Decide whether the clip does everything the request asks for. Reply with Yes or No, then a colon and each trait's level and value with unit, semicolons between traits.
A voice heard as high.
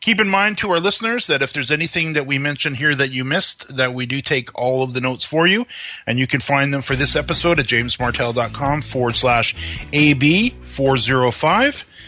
No: medium, 140 Hz